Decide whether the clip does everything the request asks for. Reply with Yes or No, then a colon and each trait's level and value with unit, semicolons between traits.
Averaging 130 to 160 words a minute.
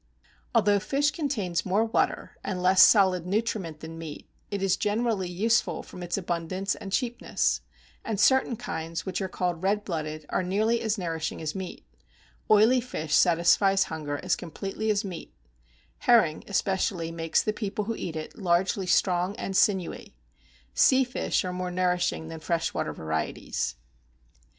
Yes: average, 155 wpm